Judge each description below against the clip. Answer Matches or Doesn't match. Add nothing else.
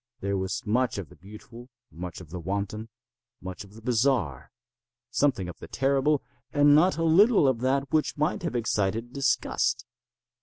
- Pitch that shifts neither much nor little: Doesn't match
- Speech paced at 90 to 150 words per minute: Doesn't match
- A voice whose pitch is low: Matches